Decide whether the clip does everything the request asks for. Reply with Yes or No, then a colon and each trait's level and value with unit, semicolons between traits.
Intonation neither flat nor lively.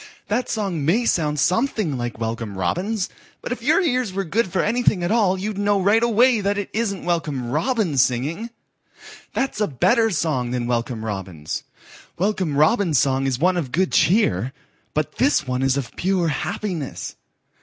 No: wide, 8.1 semitones